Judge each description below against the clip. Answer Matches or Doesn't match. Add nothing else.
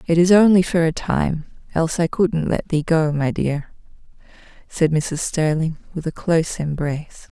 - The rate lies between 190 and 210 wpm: Doesn't match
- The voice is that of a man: Doesn't match